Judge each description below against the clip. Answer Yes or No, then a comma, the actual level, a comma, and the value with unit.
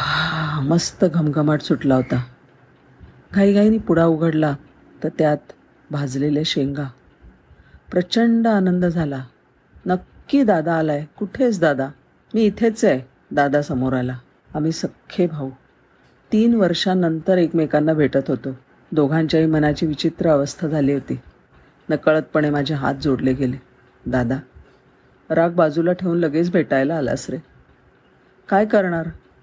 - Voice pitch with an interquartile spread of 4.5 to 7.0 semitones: No, average, 4.1 semitones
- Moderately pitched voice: Yes, medium, 155 Hz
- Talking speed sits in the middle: Yes, average, 110 wpm